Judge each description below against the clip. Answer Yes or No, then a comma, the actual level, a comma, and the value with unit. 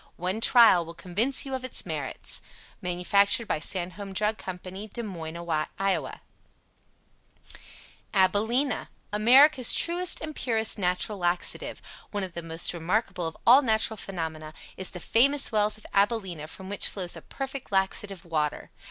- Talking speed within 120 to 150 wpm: Yes, average, 145 wpm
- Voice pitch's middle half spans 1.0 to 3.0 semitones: No, average, 4.5 semitones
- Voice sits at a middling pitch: No, high, 200 Hz